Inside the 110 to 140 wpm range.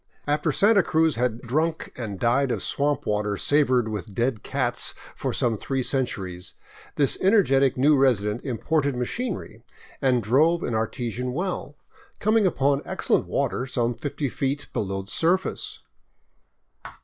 Yes: slow, 135 wpm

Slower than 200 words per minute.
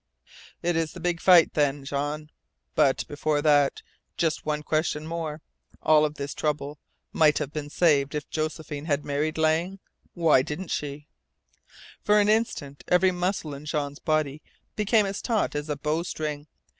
Yes: average, 155 wpm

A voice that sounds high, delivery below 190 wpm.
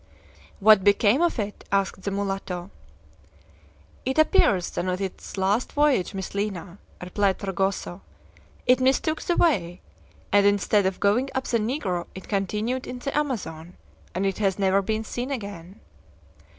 Yes: high, 200 Hz; average, 150 wpm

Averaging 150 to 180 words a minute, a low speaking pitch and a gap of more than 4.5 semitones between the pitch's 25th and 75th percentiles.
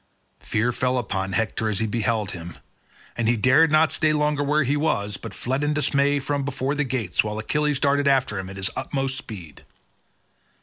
No: average, 190 wpm; low, 130 Hz; average, 5.2 semitones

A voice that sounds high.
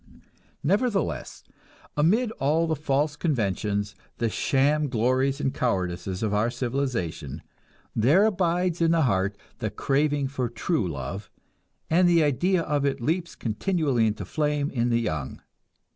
No: low, 135 Hz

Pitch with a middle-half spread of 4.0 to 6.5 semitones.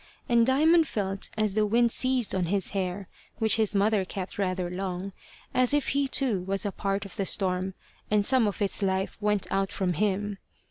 No: average, 2.7 semitones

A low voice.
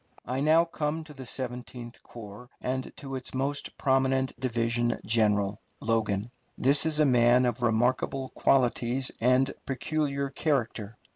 Yes: low, 130 Hz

